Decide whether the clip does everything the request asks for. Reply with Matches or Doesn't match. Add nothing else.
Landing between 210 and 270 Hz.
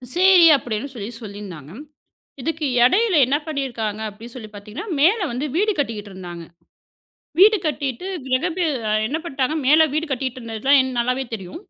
Matches